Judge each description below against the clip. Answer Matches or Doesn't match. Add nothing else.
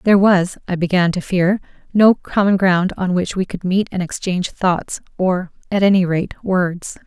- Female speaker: Matches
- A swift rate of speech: Doesn't match